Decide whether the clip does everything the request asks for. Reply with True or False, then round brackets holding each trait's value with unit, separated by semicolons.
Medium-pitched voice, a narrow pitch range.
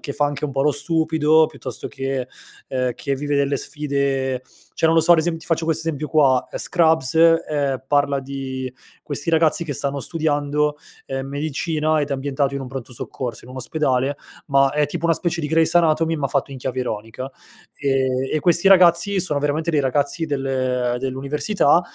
False (145 Hz; 3.0 semitones)